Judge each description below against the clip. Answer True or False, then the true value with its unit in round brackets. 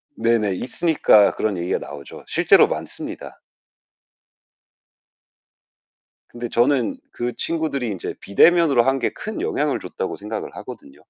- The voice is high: False (120 Hz)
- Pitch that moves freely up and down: False (4.9 semitones)